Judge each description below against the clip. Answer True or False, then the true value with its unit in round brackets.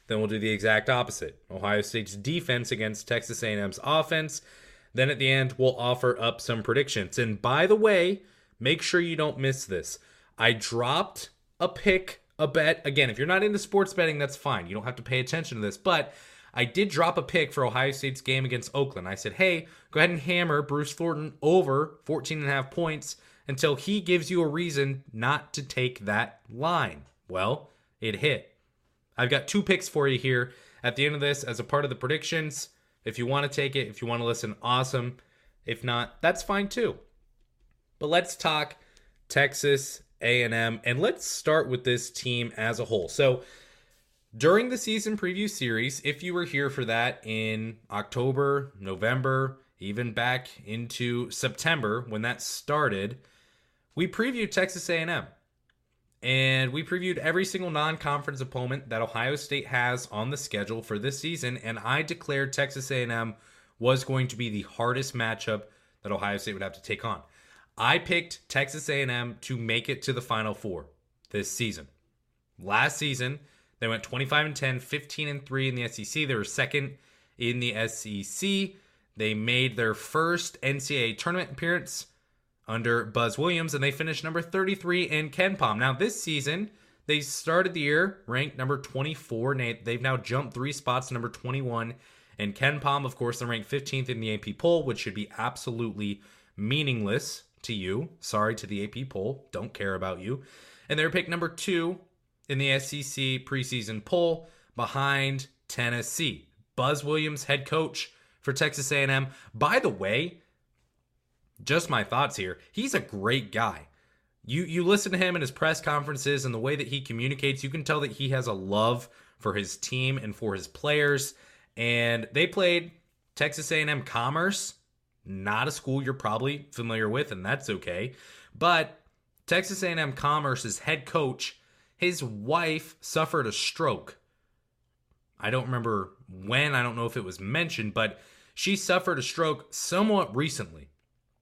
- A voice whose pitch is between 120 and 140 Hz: True (135 Hz)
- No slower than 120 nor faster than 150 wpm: False (175 wpm)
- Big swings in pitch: False (4.9 semitones)